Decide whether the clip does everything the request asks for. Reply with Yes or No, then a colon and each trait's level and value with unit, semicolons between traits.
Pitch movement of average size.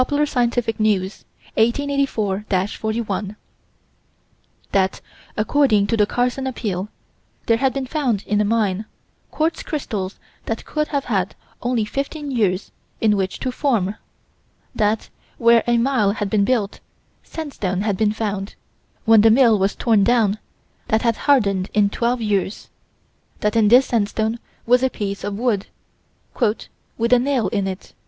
Yes: average, 3.5 semitones